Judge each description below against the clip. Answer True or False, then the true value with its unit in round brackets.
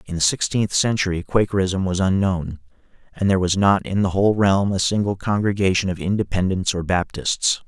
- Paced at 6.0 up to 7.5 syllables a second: False (5.4 syllables/s)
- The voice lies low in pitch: True (95 Hz)